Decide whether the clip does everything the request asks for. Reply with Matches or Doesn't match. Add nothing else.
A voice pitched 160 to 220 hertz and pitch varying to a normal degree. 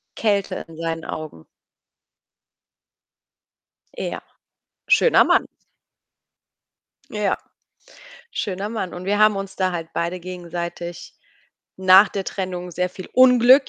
Matches